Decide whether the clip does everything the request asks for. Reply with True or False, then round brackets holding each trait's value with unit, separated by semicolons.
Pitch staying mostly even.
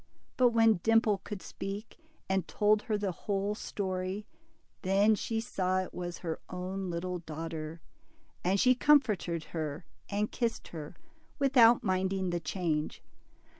False (3.5 semitones)